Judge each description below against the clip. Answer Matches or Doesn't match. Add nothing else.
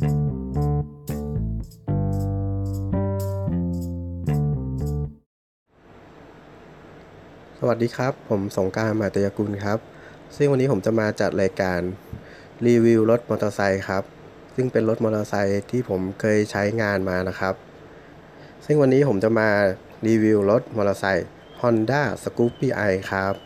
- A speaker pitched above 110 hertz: Doesn't match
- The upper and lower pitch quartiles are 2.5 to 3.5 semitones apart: Matches